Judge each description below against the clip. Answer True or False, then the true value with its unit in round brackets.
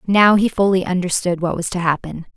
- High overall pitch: False (180 Hz)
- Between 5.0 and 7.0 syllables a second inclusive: True (5.5 syllables/s)